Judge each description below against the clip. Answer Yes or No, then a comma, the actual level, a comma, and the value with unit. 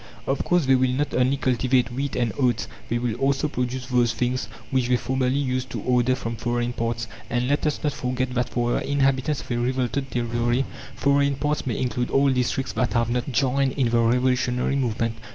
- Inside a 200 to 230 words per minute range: Yes, fast, 205 wpm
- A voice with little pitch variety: Yes, narrow, 1.9 semitones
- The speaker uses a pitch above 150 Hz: No, low, 125 Hz